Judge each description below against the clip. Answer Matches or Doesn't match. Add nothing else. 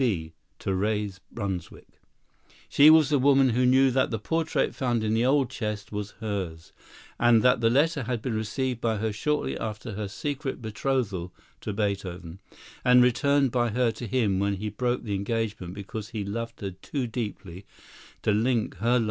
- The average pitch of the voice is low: Matches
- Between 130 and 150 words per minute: Doesn't match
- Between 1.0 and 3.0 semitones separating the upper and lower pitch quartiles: Doesn't match